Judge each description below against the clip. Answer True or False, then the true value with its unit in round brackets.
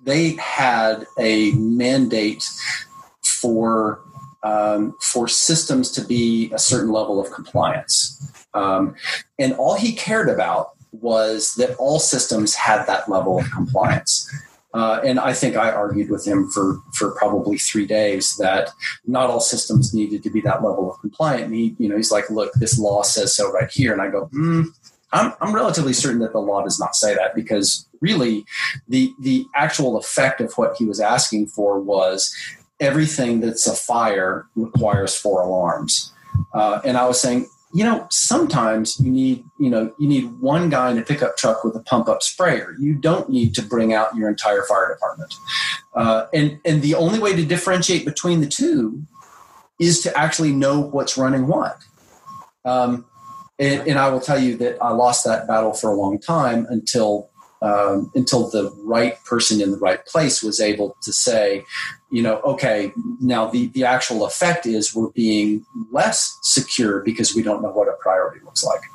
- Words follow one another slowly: False (180 wpm)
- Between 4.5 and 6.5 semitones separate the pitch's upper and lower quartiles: True (5.3 semitones)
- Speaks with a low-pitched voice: True (120 Hz)